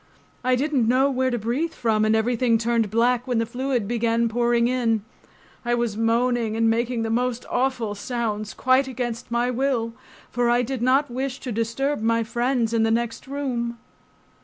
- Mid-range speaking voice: No, high, 240 Hz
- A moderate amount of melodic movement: No, narrow, 1.8 semitones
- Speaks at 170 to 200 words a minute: Yes, average, 180 wpm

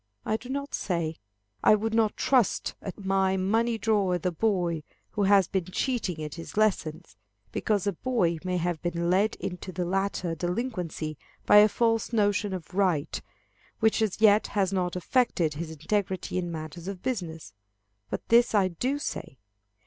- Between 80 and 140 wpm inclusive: No, average, 165 wpm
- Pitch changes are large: No, average, 3.9 semitones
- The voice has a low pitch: No, high, 190 Hz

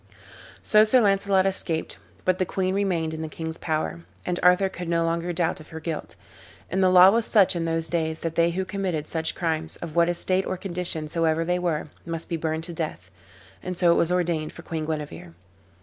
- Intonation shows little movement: Yes, narrow, 2.3 semitones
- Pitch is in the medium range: Yes, medium, 170 Hz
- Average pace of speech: No, fast, 210 wpm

